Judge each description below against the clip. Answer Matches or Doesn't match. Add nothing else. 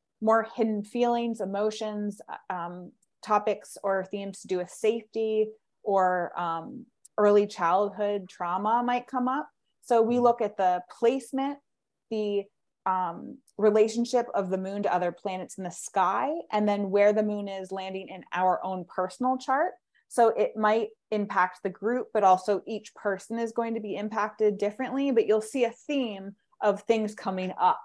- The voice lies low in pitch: Doesn't match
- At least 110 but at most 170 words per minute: Matches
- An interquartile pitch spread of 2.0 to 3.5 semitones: Matches